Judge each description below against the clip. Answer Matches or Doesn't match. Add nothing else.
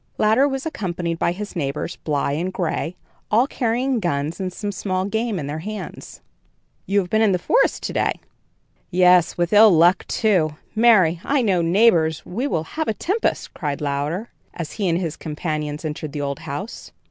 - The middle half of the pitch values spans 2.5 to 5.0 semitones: Doesn't match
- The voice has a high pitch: Doesn't match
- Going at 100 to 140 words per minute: Doesn't match